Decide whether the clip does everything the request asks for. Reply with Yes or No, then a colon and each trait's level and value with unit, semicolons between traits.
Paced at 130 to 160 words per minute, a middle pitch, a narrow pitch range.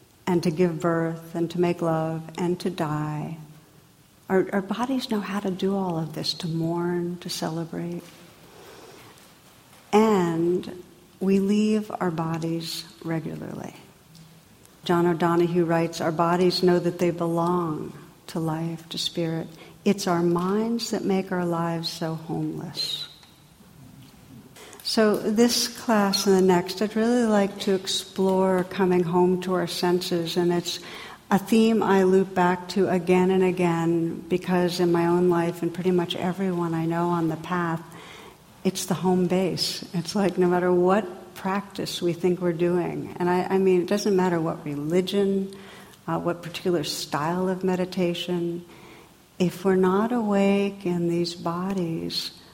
Yes: average, 150 wpm; medium, 180 Hz; narrow, 1.9 semitones